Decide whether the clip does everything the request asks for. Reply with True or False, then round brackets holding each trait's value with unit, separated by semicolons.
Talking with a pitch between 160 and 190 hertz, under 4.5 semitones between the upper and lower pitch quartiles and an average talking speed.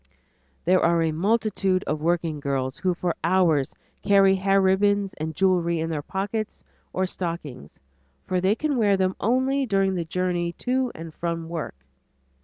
True (185 Hz; 3.1 semitones; 160 wpm)